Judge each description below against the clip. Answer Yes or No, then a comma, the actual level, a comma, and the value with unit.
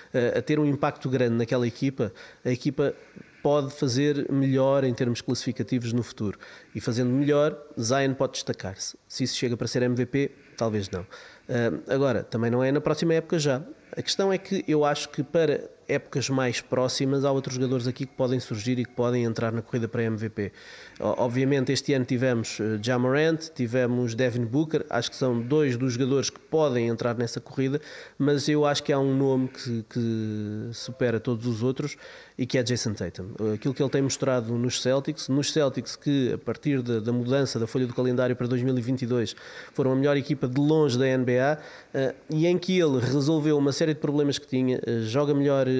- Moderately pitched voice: No, low, 130 Hz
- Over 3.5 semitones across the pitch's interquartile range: No, average, 2.9 semitones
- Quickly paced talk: Yes, fast, 190 wpm